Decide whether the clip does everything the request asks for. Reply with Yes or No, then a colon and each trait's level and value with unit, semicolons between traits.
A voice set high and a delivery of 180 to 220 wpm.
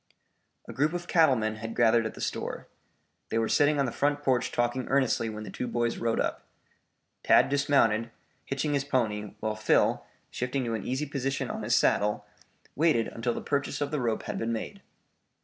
No: low, 125 Hz; average, 195 wpm